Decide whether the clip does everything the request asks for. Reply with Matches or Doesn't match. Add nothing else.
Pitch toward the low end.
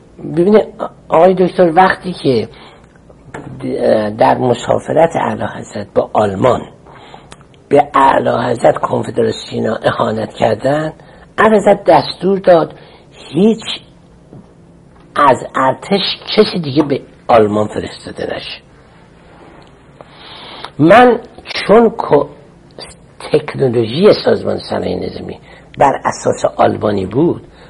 Doesn't match